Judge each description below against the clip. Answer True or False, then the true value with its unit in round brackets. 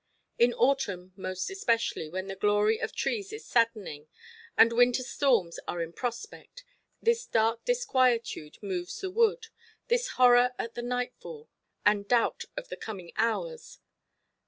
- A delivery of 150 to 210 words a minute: False (140 wpm)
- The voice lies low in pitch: False (235 Hz)